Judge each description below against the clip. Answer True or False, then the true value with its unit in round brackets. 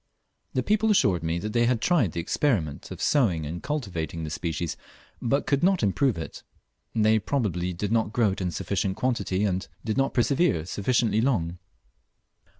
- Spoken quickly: False (165 wpm)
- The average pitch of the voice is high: False (105 Hz)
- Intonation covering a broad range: True (6.7 semitones)